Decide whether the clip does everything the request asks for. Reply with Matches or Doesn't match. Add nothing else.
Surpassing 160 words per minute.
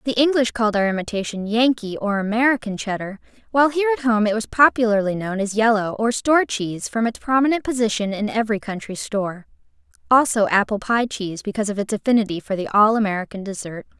Matches